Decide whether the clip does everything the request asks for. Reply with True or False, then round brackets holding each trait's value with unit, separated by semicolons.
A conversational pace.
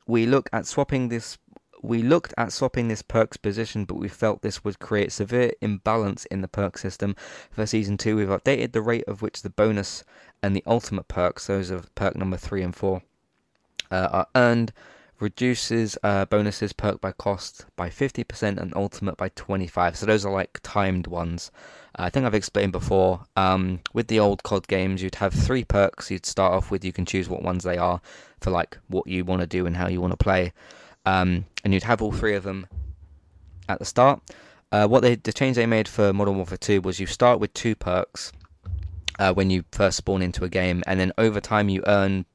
False (210 wpm)